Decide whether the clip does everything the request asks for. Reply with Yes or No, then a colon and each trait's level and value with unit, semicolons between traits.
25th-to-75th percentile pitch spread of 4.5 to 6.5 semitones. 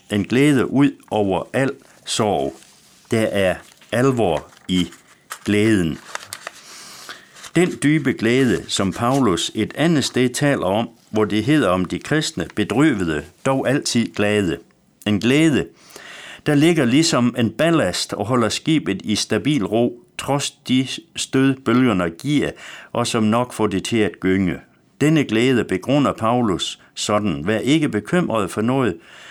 Yes: average, 5.3 semitones